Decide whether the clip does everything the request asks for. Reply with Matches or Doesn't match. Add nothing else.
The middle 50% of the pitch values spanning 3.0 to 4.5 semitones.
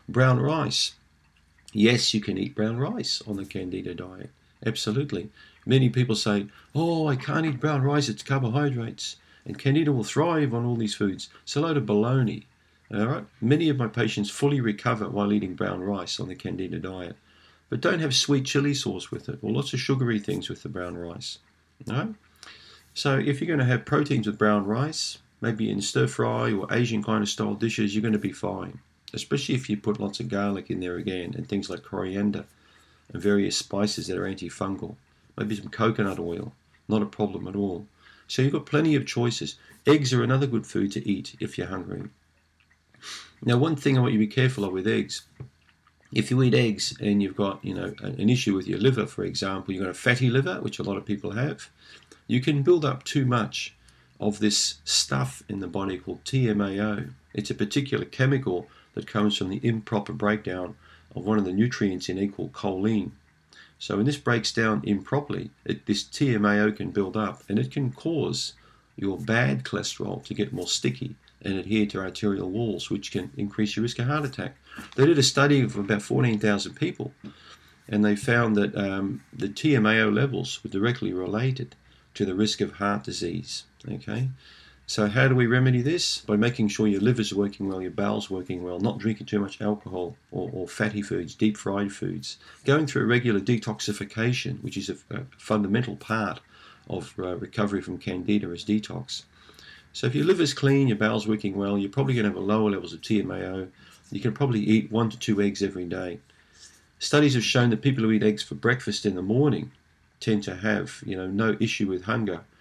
Matches